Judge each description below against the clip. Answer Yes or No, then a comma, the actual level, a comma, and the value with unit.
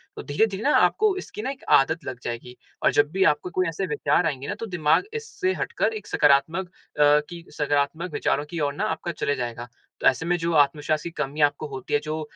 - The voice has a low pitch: No, medium, 155 Hz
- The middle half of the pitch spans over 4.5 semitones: No, average, 3.9 semitones